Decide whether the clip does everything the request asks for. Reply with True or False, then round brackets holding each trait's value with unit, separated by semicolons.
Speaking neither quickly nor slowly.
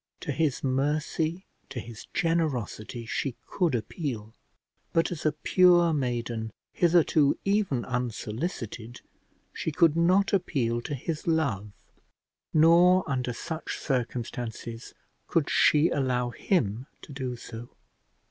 False (115 wpm)